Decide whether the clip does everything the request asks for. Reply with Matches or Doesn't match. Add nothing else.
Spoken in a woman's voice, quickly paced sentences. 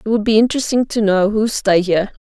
Matches